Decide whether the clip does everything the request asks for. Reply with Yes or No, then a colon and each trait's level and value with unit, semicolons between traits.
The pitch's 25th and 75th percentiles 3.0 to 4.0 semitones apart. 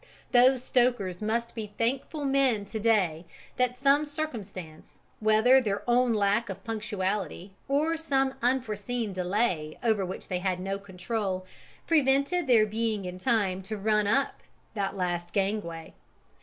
No: average, 4.5 semitones